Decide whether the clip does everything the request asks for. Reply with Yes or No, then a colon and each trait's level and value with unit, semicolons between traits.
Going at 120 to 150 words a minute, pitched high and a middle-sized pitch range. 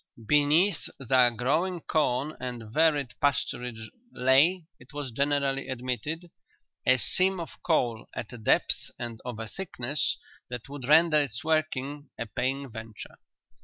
No: slow, 135 wpm; low, 135 Hz; average, 4.0 semitones